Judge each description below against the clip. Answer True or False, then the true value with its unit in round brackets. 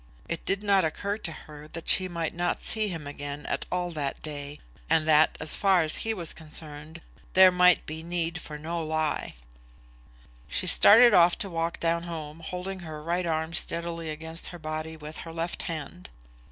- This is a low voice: False (165 Hz)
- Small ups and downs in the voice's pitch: True (2.2 semitones)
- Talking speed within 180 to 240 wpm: True (185 wpm)